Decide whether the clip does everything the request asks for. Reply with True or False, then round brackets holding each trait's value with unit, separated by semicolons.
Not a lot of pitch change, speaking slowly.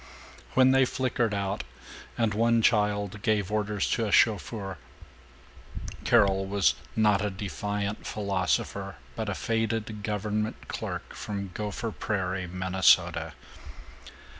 True (2.0 semitones; 115 wpm)